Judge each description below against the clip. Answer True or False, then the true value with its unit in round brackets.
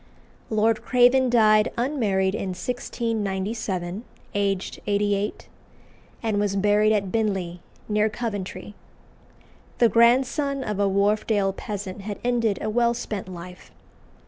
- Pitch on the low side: False (210 Hz)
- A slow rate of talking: True (115 wpm)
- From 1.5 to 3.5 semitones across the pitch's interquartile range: True (2.8 semitones)